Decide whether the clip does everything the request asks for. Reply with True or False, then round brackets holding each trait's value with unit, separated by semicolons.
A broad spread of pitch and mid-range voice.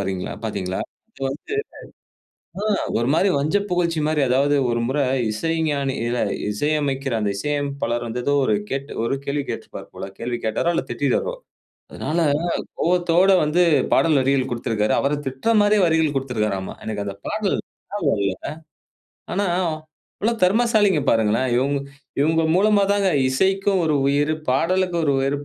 True (6.3 semitones; 145 Hz)